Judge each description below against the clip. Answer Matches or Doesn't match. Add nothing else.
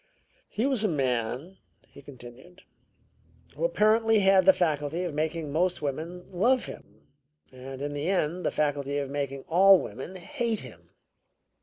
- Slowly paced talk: Doesn't match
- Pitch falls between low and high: Matches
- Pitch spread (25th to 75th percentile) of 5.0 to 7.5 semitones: Matches